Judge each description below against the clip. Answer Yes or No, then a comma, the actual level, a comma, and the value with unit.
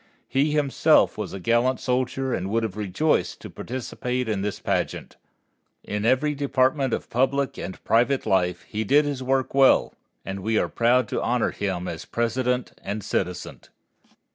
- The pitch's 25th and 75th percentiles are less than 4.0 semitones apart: No, average, 4.3 semitones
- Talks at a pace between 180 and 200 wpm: No, average, 165 wpm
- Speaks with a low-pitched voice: Yes, low, 120 Hz